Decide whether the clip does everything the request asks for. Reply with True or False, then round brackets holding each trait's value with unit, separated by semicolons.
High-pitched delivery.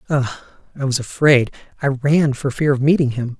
False (135 Hz)